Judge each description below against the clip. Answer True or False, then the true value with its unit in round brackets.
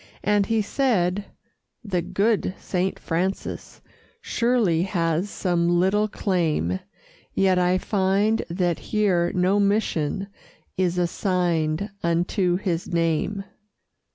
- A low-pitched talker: False (185 Hz)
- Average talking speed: False (100 wpm)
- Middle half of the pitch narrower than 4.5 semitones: True (2.8 semitones)